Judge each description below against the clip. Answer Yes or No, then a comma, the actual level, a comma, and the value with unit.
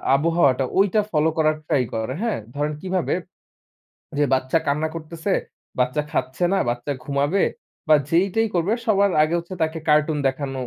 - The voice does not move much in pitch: No, average, 4.1 semitones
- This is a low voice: No, medium, 155 Hz